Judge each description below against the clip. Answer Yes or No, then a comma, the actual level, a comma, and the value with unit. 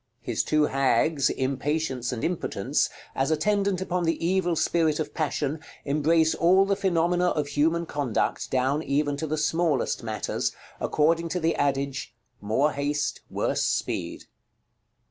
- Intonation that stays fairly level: No, average, 3.2 semitones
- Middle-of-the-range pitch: Yes, medium, 155 Hz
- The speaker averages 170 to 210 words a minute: No, average, 140 wpm